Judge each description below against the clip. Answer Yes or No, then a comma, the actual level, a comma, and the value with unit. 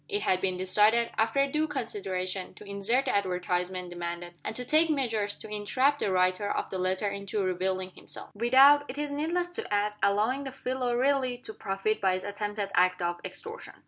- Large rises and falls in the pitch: Yes, wide, 5.8 semitones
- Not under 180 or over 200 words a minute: Yes, average, 190 wpm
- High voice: Yes, high, 205 Hz